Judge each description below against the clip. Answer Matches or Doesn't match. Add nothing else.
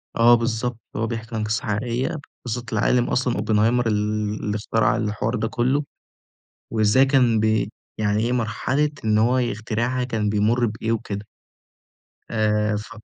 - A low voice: Matches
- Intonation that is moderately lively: Doesn't match